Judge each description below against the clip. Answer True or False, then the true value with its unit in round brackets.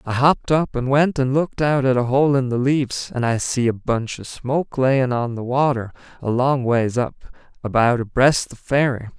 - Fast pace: True (215 wpm)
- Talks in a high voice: False (130 Hz)